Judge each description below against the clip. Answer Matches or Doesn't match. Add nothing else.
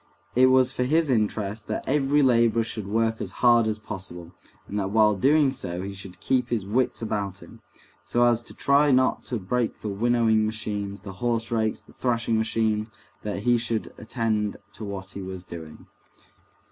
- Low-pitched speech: Matches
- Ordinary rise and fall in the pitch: Matches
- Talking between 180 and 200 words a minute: Matches